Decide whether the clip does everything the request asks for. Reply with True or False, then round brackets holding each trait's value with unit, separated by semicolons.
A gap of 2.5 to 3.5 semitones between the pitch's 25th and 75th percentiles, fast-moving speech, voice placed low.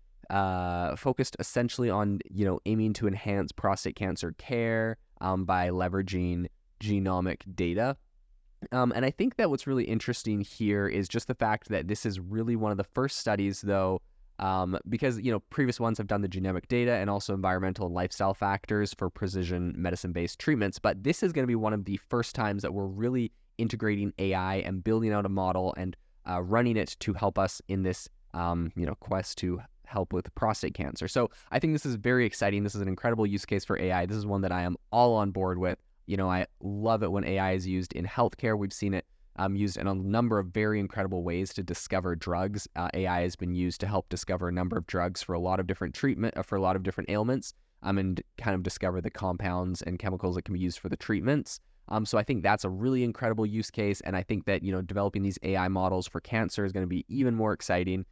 True (3.0 semitones; 230 wpm; 100 Hz)